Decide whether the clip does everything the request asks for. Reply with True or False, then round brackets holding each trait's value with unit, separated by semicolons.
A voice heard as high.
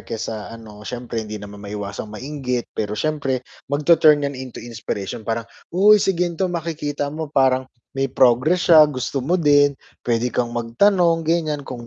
False (135 Hz)